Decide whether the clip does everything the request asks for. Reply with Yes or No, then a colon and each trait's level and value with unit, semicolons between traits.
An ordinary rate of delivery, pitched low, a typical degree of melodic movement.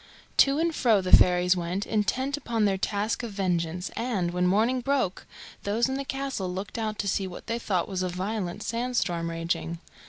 No: average, 195 wpm; high, 200 Hz; average, 4.7 semitones